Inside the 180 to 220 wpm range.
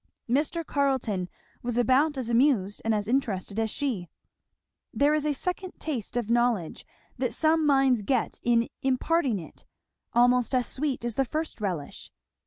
No: average, 155 wpm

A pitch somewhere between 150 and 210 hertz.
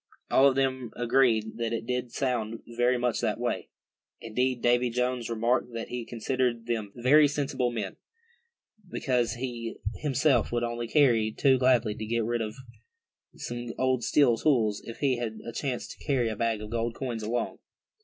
No: low, 120 Hz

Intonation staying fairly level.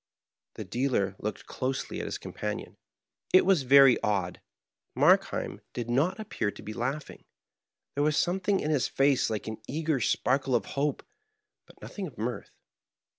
No: average, 4.4 semitones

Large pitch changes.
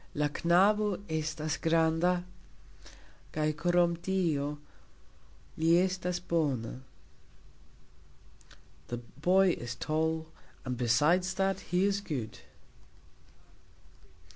No: average, 3.4 semitones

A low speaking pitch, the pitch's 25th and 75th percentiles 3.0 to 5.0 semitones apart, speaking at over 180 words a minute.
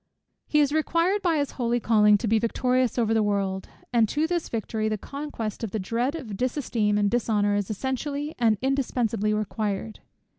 No: high, 230 Hz; average, 4.6 semitones; average, 190 wpm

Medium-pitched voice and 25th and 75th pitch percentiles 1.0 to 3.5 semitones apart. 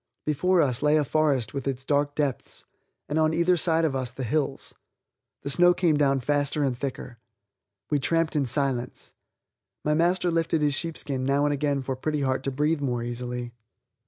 Yes: medium, 145 Hz; average, 2.9 semitones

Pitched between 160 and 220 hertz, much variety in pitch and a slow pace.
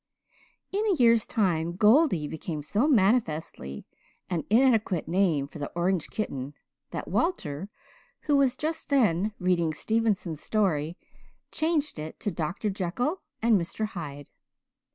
Yes: high, 190 Hz; wide, 6.6 semitones; slow, 130 wpm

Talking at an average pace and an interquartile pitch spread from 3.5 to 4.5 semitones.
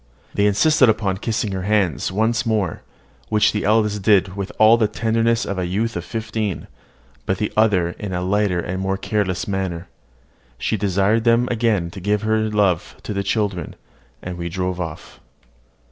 No: average, 175 wpm; average, 2.9 semitones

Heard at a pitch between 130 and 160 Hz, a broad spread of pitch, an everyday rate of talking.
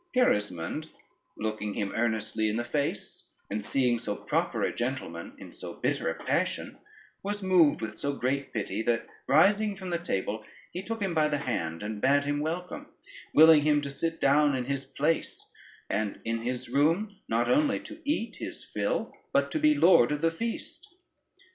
Yes: medium, 140 Hz; wide, 7.4 semitones; average, 175 wpm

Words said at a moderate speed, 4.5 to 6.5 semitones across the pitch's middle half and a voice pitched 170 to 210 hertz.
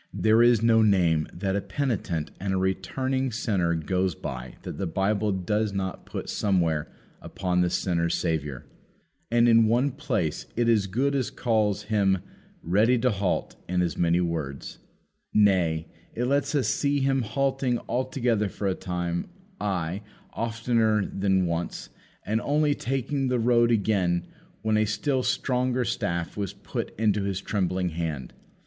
No: average, 155 wpm; average, 5.1 semitones; low, 105 Hz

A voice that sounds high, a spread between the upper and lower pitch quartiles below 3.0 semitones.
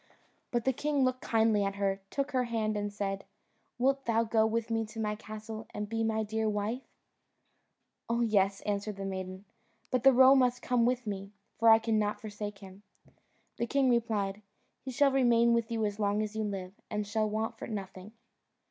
Yes: high, 220 Hz; narrow, 2.4 semitones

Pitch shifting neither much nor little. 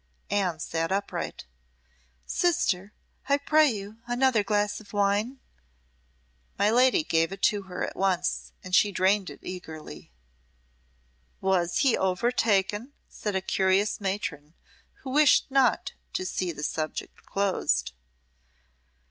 Yes: average, 4.0 semitones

